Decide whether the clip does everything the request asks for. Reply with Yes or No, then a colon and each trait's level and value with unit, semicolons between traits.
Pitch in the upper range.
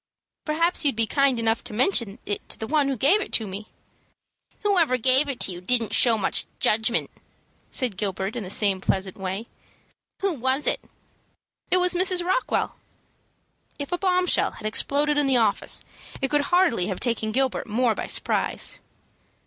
Yes: very high, 250 Hz